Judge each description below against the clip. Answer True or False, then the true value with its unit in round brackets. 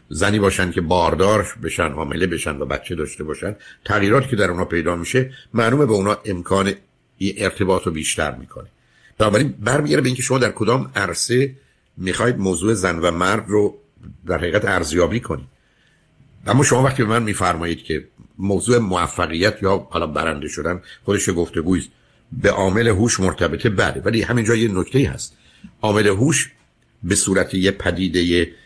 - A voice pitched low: True (100 Hz)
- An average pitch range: True (4.9 semitones)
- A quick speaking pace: True (160 wpm)